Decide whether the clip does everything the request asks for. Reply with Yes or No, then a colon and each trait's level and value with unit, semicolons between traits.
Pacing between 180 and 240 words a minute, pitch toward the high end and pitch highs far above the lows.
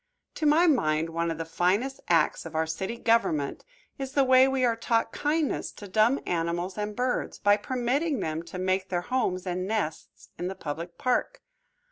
Yes: average, 185 wpm; high, 205 Hz; wide, 7.1 semitones